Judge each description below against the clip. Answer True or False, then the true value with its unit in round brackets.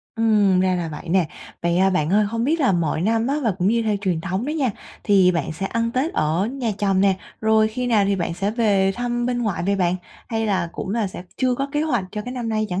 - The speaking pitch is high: True (210 Hz)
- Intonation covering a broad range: False (3.9 semitones)